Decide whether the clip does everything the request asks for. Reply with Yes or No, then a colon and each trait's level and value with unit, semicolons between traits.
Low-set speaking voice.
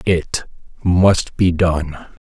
Yes: very low, 85 Hz